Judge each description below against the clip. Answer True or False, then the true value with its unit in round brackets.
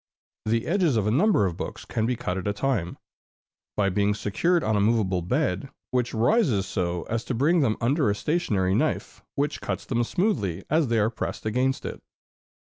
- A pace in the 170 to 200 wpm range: True (195 wpm)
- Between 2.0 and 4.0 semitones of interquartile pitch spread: False (5.3 semitones)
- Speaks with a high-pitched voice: False (115 Hz)